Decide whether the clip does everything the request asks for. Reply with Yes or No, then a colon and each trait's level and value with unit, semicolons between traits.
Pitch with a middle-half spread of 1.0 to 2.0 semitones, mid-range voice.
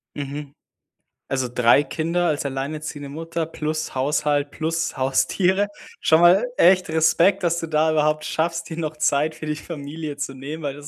No: narrow, 2.4 semitones; medium, 155 Hz